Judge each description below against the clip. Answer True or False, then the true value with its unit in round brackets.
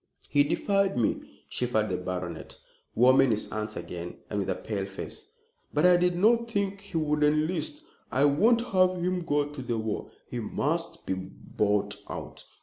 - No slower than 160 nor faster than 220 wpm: True (170 wpm)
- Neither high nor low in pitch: True (145 Hz)